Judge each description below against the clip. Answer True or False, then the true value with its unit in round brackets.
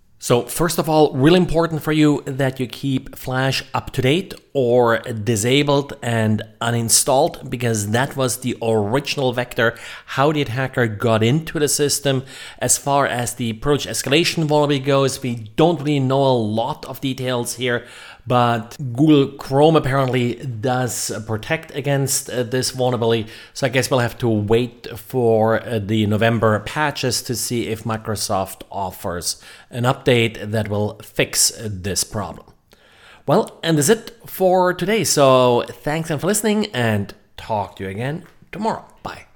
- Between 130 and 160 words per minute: True (150 wpm)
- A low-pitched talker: True (130 Hz)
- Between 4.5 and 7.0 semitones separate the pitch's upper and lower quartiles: False (3.9 semitones)